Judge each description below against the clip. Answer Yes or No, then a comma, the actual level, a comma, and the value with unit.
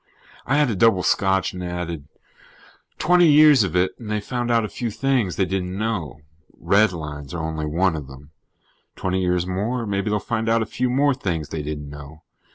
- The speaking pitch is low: Yes, very low, 95 Hz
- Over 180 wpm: Yes, average, 195 wpm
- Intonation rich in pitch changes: Yes, wide, 6.0 semitones